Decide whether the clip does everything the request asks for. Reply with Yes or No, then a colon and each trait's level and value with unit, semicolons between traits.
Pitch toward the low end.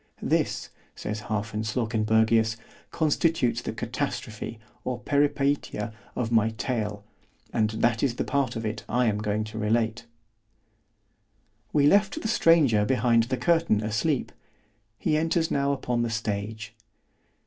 Yes: low, 115 Hz